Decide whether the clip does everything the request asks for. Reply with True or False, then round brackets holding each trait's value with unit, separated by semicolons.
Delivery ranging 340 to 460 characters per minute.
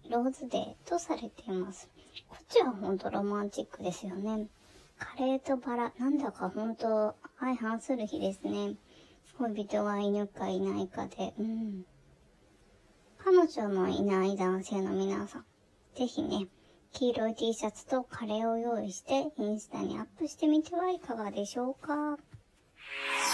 False (290 characters per minute)